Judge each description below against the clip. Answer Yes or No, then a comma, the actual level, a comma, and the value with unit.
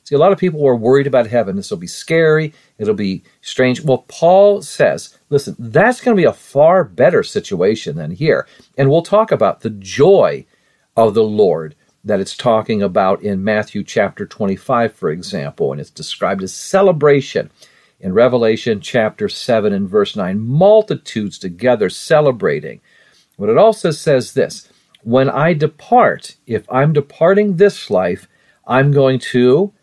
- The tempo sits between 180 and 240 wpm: No, average, 160 wpm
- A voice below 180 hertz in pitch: Yes, medium, 140 Hz